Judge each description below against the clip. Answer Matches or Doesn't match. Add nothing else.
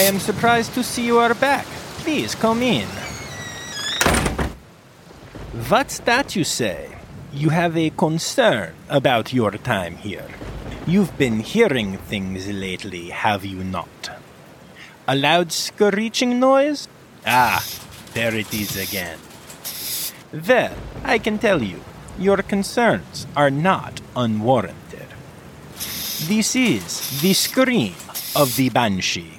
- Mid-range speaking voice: Matches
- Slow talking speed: Matches